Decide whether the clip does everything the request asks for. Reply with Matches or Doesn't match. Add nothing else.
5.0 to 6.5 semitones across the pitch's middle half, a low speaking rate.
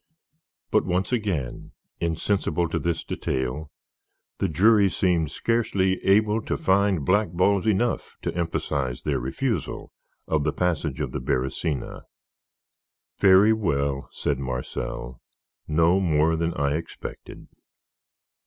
Matches